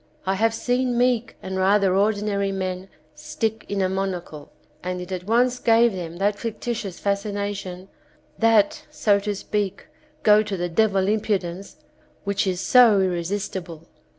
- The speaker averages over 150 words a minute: No, average, 145 wpm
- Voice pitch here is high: Yes, high, 200 Hz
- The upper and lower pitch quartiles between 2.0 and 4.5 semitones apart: Yes, narrow, 2.5 semitones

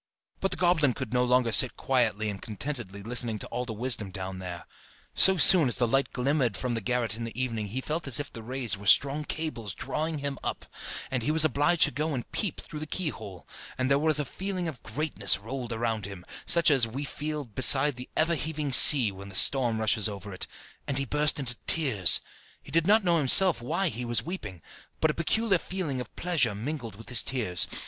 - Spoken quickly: Yes, fast, 215 wpm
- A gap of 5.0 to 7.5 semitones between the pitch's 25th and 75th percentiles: Yes, average, 5.3 semitones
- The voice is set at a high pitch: No, low, 130 Hz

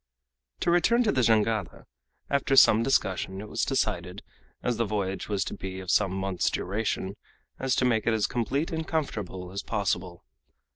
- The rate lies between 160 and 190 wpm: Yes, average, 165 wpm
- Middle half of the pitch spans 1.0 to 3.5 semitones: No, average, 5.2 semitones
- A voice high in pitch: No, low, 105 Hz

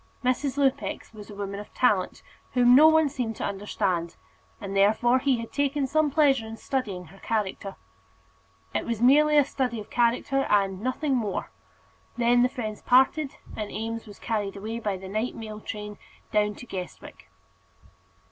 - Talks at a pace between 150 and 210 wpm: Yes, average, 165 wpm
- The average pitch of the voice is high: Yes, high, 230 Hz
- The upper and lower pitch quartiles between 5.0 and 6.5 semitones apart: No, average, 4.2 semitones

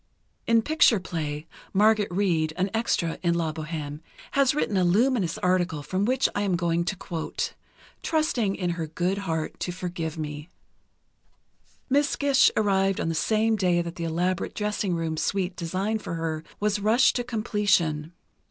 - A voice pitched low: No, medium, 185 Hz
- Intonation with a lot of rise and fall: No, average, 4.3 semitones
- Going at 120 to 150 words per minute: No, average, 160 wpm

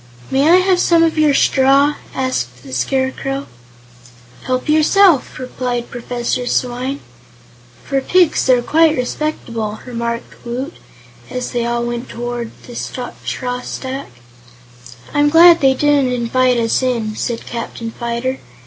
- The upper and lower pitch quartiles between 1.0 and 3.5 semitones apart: Yes, average, 3.1 semitones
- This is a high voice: Yes, very high, 255 Hz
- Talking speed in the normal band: No, slow, 130 wpm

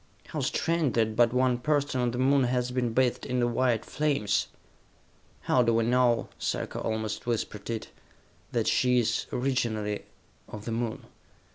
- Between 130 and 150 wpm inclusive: No, average, 160 wpm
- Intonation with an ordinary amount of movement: No, narrow, 2.1 semitones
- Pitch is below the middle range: Yes, low, 120 Hz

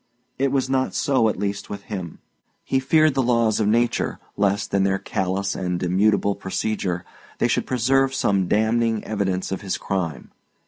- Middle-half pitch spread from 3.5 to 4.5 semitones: Yes, average, 4.0 semitones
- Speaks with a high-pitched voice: No, low, 105 Hz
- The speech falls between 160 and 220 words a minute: Yes, average, 170 wpm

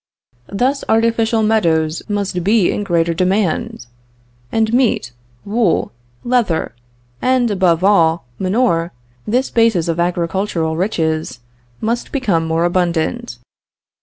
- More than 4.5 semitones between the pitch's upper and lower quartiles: Yes, average, 5.2 semitones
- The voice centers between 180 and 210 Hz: Yes, high, 190 Hz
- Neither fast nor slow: No, slow, 105 wpm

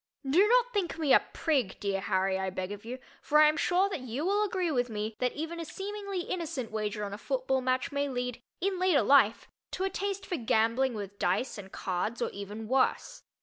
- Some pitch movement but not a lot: No, wide, 8.5 semitones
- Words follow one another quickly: Yes, fast, 220 wpm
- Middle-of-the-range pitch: No, very high, 260 Hz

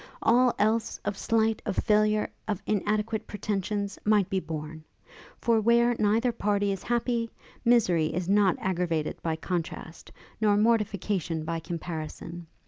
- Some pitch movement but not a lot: Yes, average, 4.0 semitones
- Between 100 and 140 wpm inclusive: Yes, slow, 135 wpm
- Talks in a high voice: Yes, high, 205 Hz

